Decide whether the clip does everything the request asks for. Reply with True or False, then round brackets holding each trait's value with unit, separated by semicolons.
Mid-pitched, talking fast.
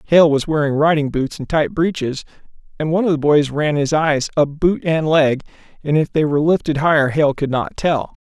True (150 Hz; 220 wpm)